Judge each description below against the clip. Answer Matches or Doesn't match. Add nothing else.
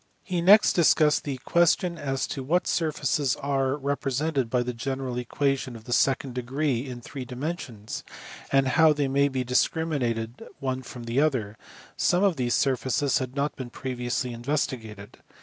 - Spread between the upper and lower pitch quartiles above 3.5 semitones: Doesn't match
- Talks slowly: Doesn't match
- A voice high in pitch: Doesn't match